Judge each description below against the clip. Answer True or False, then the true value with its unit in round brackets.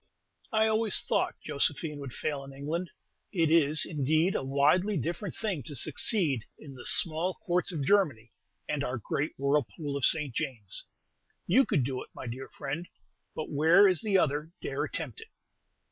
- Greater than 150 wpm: True (170 wpm)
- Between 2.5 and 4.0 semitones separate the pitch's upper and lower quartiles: False (4.5 semitones)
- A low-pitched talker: False (155 Hz)